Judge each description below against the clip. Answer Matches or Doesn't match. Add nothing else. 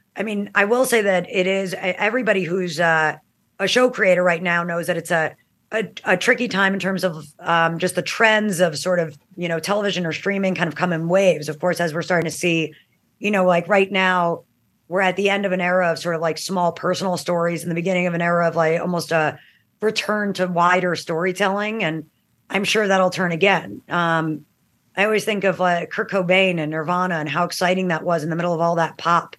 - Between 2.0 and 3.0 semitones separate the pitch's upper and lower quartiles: Matches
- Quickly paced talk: Matches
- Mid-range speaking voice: Matches